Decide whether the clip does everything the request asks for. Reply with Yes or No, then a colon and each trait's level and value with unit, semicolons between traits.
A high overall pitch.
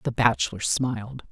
No: low, 110 Hz